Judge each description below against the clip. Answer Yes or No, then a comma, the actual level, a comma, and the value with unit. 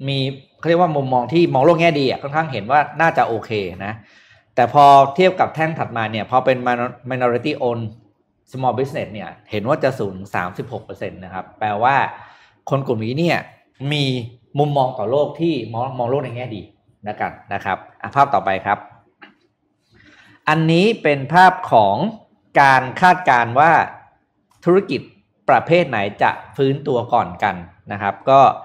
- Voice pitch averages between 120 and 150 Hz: Yes, low, 135 Hz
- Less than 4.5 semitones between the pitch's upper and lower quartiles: No, average, 5.2 semitones